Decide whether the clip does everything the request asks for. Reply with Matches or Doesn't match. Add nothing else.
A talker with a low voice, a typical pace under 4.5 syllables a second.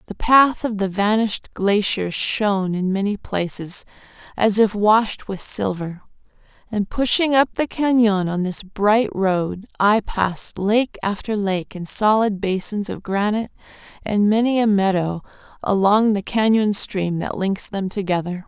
Doesn't match